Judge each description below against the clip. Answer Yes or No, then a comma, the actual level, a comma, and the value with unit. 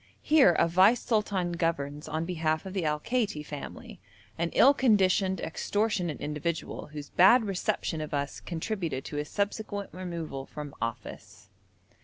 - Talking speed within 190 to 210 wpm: No, average, 145 wpm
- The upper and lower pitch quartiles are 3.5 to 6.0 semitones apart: Yes, average, 5.0 semitones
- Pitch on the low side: No, medium, 170 Hz